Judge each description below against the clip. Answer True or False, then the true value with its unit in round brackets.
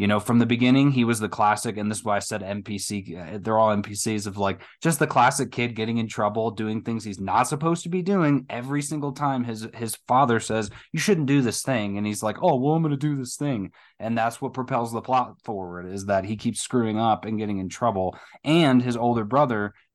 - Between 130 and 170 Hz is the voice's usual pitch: False (115 Hz)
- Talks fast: True (240 wpm)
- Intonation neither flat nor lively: True (4.1 semitones)